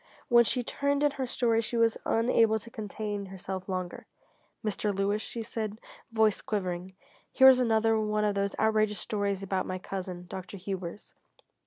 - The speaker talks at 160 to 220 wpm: Yes, average, 165 wpm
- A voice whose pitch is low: No, high, 210 Hz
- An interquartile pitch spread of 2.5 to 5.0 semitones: Yes, average, 2.8 semitones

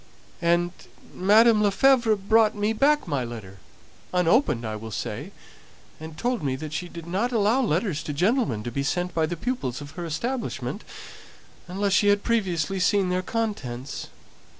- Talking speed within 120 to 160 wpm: Yes, average, 155 wpm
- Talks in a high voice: No, medium, 180 Hz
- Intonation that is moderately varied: No, wide, 6.7 semitones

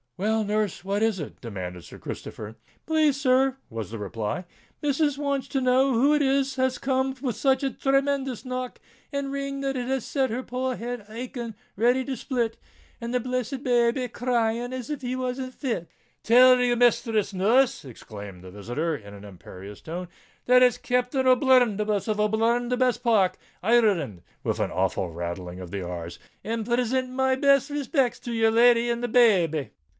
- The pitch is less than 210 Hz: No, high, 240 Hz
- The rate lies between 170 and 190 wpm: Yes, average, 180 wpm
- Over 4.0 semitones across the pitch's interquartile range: Yes, average, 4.7 semitones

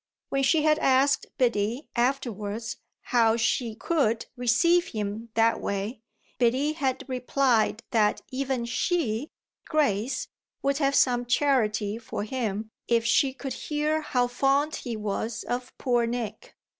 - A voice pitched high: Yes, high, 245 Hz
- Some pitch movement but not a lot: Yes, average, 3.5 semitones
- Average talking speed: No, slow, 130 wpm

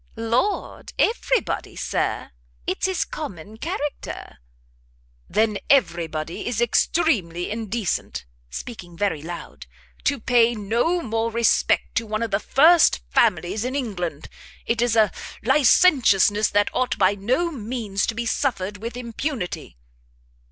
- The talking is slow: Yes, slow, 130 wpm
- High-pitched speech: Yes, high, 225 Hz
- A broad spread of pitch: No, average, 4.5 semitones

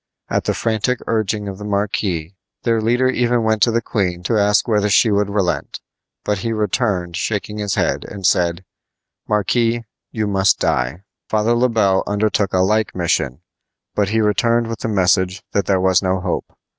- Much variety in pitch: No, average, 3.0 semitones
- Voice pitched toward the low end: Yes, low, 105 Hz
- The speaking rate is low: No, average, 175 wpm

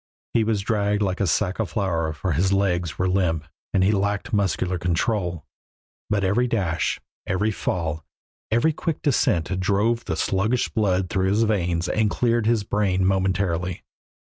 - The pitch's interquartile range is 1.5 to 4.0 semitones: Yes, average, 2.9 semitones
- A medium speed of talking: Yes, average, 160 wpm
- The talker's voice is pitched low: Yes, very low, 95 Hz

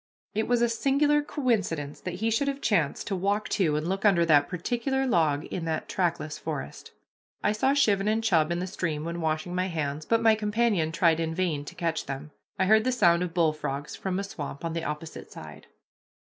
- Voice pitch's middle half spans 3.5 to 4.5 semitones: No, wide, 5.5 semitones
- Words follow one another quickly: Yes, fast, 210 wpm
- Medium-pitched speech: Yes, medium, 180 Hz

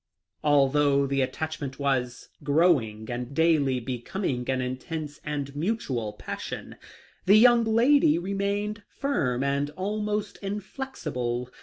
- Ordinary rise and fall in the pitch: No, wide, 7.5 semitones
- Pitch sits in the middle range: Yes, medium, 145 Hz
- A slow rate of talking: Yes, slow, 110 wpm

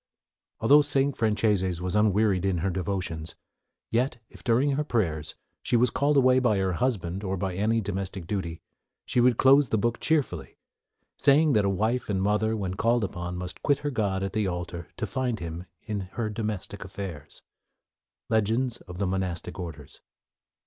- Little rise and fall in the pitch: No, average, 4.6 semitones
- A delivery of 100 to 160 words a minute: No, average, 170 wpm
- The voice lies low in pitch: Yes, low, 105 Hz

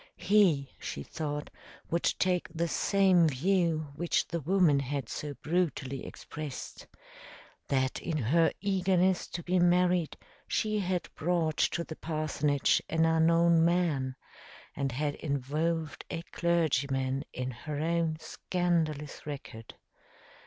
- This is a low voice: No, medium, 160 Hz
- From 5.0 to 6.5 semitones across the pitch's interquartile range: No, average, 3.5 semitones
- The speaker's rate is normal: No, slow, 120 wpm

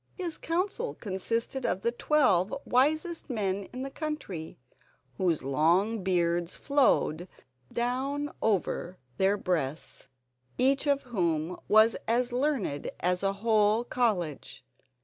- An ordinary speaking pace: No, slow, 115 wpm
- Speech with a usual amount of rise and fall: No, wide, 6.7 semitones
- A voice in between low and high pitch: No, high, 215 Hz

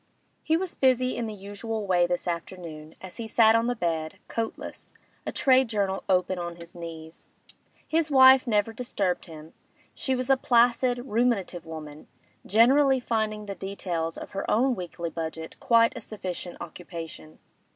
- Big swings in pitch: Yes, wide, 6.0 semitones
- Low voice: No, high, 205 Hz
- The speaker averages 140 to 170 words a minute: Yes, average, 160 wpm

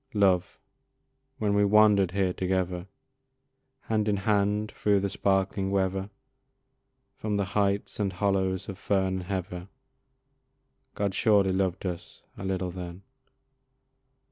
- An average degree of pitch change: No, narrow, 1.5 semitones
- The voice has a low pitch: Yes, very low, 95 Hz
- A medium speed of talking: No, slow, 120 wpm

